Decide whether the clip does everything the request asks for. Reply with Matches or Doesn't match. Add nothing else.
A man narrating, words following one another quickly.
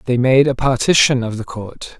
Matches